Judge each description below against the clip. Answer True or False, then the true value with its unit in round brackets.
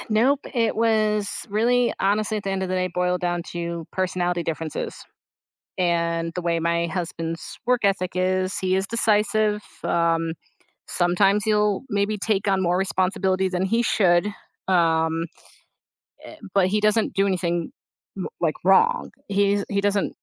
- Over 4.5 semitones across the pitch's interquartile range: False (3.2 semitones)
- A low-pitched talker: False (190 Hz)